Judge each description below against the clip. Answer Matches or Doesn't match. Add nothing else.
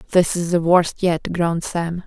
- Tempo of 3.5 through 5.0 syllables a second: Matches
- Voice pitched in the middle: Matches